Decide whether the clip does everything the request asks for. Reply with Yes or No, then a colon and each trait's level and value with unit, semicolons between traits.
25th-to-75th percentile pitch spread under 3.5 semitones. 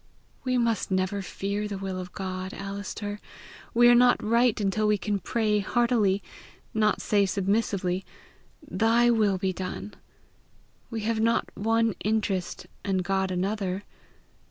Yes: average, 2.7 semitones